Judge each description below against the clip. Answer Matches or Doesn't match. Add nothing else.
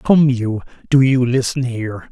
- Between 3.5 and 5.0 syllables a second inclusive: Matches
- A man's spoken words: Matches